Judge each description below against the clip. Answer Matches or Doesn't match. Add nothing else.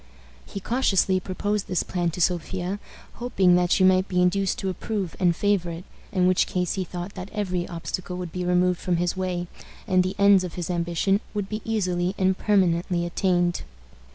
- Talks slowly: Doesn't match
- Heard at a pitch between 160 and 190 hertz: Matches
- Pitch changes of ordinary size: Doesn't match